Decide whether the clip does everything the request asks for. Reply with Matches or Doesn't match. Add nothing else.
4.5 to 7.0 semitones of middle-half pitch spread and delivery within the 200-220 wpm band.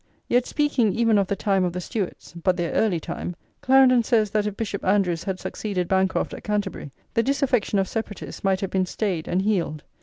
Doesn't match